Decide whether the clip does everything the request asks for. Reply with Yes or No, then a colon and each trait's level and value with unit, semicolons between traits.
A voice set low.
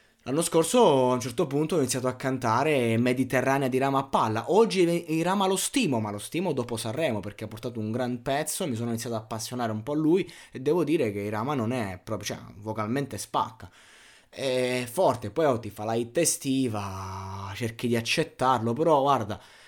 Yes: low, 125 Hz